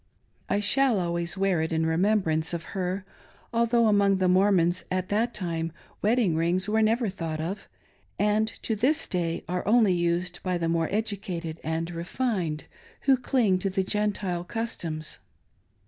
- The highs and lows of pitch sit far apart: No, average, 3.8 semitones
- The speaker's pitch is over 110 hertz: Yes, medium, 185 Hz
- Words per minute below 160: Yes, average, 150 wpm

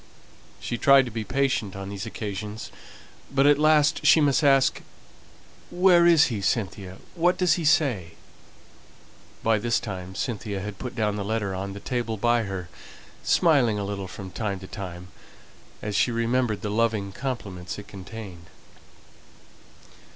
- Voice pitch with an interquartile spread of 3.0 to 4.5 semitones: No, average, 5.2 semitones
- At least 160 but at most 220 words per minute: No, average, 150 wpm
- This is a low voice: Yes, low, 110 Hz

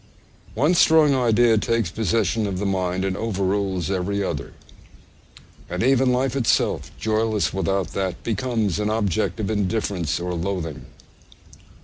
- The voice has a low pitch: Yes, low, 105 Hz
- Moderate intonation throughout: Yes, average, 3.4 semitones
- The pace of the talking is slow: Yes, slow, 130 wpm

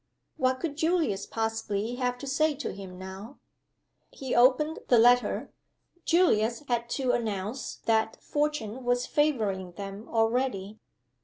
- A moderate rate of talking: No, slow, 130 wpm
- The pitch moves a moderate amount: Yes, average, 4.4 semitones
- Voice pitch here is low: No, high, 240 Hz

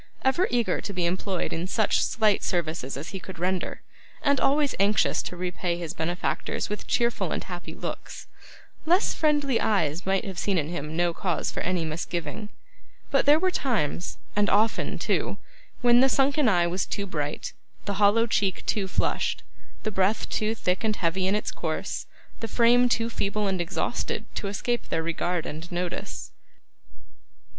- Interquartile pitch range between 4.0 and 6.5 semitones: Yes, average, 4.7 semitones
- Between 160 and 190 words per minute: Yes, average, 170 wpm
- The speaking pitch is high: Yes, high, 195 Hz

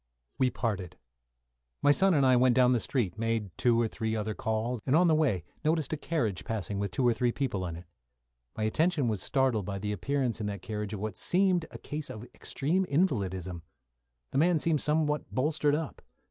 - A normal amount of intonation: No, wide, 6.0 semitones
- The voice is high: No, low, 125 Hz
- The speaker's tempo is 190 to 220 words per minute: Yes, average, 200 wpm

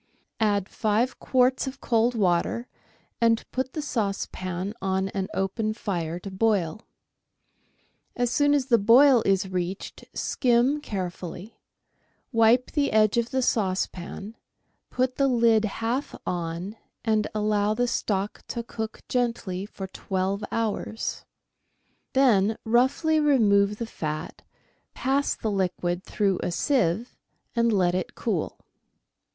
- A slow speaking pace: Yes, slow, 125 wpm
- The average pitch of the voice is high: Yes, high, 215 Hz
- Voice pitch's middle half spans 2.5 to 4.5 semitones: Yes, average, 4.1 semitones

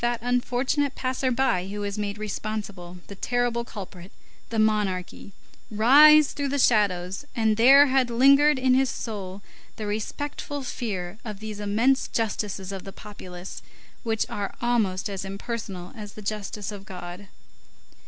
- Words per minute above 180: No, average, 145 wpm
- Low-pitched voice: No, high, 215 Hz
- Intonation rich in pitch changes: No, average, 3.9 semitones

